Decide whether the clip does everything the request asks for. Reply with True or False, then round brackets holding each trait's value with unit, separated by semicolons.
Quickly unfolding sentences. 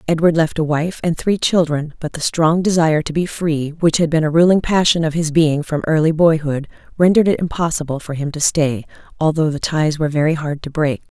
True (220 wpm)